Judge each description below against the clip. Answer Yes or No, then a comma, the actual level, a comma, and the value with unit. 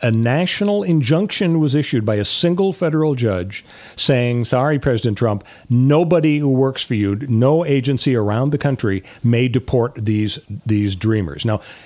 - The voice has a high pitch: No, low, 125 Hz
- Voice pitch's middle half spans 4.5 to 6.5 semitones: Yes, wide, 5.6 semitones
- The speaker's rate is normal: Yes, average, 150 wpm